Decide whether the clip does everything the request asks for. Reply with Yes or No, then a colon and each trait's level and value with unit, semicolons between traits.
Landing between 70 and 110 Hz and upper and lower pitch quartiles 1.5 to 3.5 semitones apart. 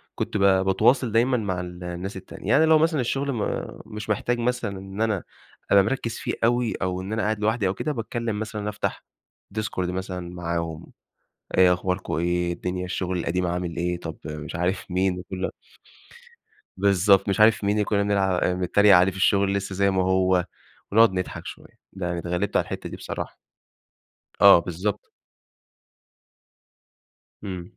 Yes: very low, 95 Hz; average, 2.9 semitones